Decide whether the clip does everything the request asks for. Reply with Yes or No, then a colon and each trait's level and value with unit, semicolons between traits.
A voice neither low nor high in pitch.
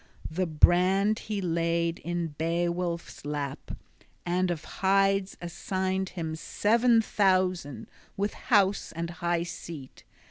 Yes: medium, 175 Hz